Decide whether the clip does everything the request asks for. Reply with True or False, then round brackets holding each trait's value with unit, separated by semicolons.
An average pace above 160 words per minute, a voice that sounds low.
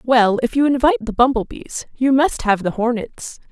False (205 wpm; 250 Hz)